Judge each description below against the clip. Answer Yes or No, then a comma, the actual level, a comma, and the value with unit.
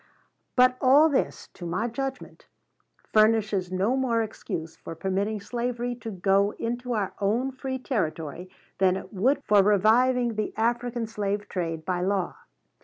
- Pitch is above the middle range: Yes, high, 215 Hz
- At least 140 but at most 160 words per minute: Yes, average, 145 wpm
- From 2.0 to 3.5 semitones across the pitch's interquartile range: No, average, 4.3 semitones